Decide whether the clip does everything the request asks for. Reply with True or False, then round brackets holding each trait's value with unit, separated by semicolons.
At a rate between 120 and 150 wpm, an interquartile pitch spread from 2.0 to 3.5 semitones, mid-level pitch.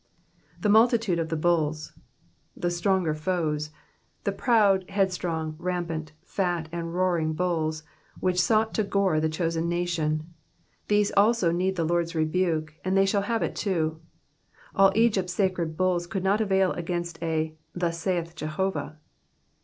True (140 wpm; 3.1 semitones; 175 Hz)